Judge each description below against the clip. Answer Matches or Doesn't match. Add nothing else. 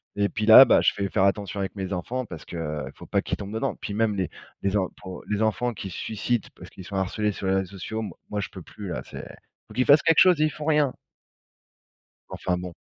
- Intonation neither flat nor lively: Matches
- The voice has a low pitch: Matches